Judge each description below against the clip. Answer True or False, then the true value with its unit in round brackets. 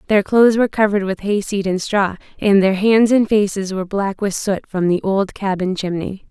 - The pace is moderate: False (210 wpm)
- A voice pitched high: True (200 Hz)